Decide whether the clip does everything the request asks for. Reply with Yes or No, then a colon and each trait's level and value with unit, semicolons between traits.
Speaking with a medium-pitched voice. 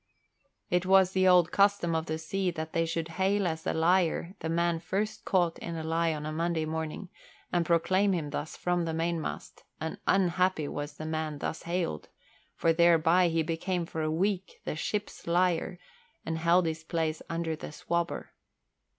Yes: medium, 170 Hz